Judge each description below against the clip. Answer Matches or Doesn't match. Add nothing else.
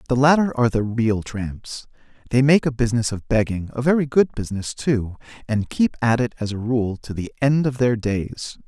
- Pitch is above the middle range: Doesn't match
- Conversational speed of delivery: Matches